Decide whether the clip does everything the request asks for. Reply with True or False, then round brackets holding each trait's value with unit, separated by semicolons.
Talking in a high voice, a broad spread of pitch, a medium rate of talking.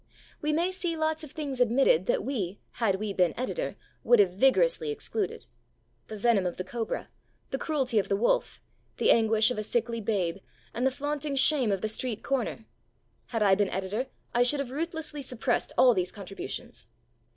True (245 Hz; 5.9 semitones; 185 wpm)